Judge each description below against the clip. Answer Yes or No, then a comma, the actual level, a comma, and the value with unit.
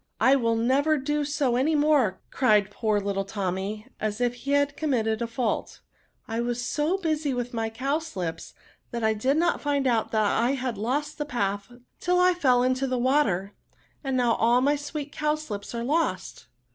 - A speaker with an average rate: Yes, average, 185 wpm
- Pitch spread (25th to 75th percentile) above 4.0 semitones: Yes, average, 4.8 semitones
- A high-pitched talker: Yes, very high, 250 Hz